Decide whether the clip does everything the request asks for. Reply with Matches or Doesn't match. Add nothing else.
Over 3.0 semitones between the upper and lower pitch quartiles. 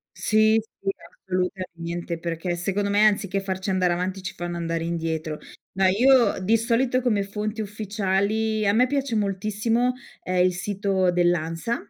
Matches